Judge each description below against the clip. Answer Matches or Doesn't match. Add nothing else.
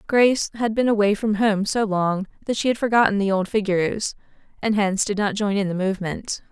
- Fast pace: Matches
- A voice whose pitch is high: Matches